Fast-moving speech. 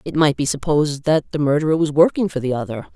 Yes: fast, 245 wpm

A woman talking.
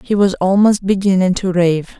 Yes: female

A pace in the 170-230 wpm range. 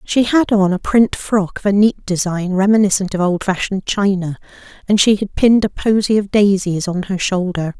Yes: average, 190 wpm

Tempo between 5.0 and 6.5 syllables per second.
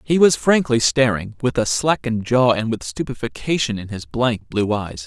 No: 4.8 syllables/s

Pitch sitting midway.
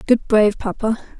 No: high, 220 Hz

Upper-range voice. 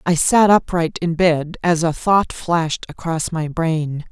No: medium, 165 Hz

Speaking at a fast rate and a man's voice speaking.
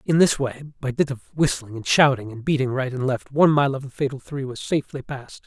Yes: fast, 255 wpm; male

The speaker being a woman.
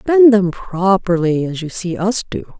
Yes: female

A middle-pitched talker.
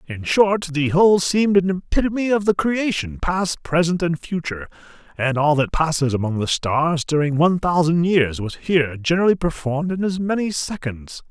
Yes: medium, 165 Hz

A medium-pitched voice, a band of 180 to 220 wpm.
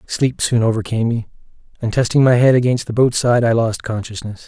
No: low, 115 Hz; average, 200 wpm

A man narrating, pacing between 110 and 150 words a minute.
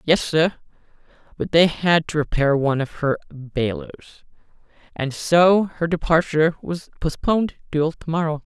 Yes: male; average, 140 wpm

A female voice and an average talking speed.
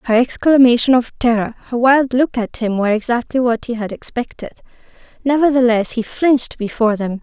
Yes: female; average, 165 wpm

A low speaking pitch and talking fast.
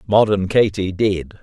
No: low, 100 Hz; slow, 125 wpm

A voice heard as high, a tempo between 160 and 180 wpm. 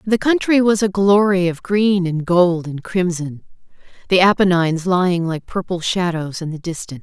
No: medium, 180 Hz; average, 170 wpm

